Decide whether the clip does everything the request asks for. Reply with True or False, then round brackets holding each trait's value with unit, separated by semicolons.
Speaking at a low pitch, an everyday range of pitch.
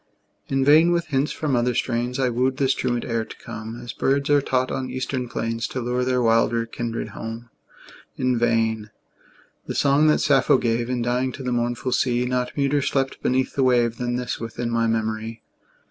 False (125 Hz; 2.2 semitones)